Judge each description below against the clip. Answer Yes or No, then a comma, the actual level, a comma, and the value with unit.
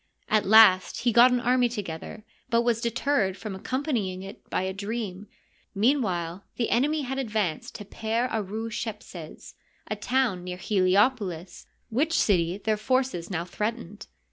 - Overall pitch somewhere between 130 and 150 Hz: No, high, 215 Hz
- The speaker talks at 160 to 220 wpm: No, average, 140 wpm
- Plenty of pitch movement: No, average, 4.2 semitones